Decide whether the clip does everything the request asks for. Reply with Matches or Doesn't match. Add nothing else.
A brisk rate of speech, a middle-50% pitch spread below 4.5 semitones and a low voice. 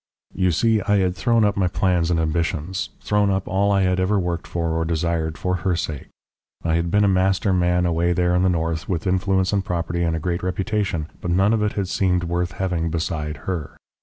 Matches